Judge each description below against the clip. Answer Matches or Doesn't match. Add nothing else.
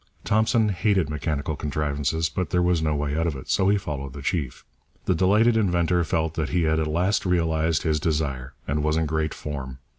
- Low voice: Matches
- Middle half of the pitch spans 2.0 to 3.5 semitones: Matches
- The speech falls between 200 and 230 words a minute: Matches